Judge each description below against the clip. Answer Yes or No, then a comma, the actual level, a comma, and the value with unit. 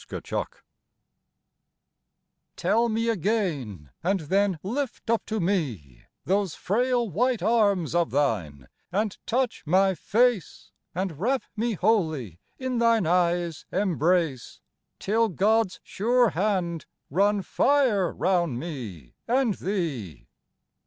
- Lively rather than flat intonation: Yes, wide, 5.7 semitones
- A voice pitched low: No, high, 190 Hz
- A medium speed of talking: No, slow, 110 wpm